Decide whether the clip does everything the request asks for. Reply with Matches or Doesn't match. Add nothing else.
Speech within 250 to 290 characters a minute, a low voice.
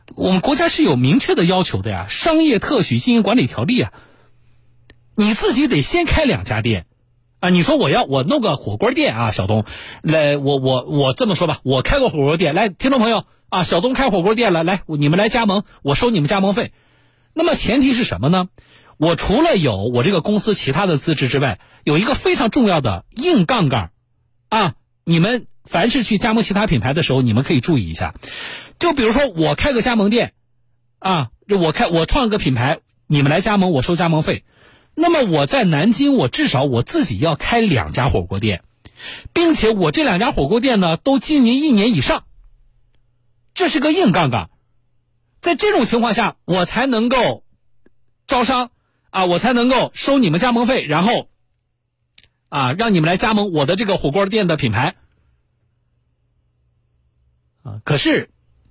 Doesn't match